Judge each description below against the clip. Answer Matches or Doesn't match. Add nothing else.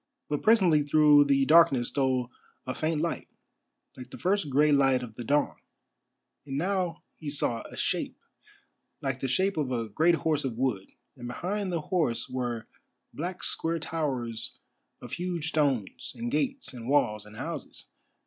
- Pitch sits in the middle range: Matches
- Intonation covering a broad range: Doesn't match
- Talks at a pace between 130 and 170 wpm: Matches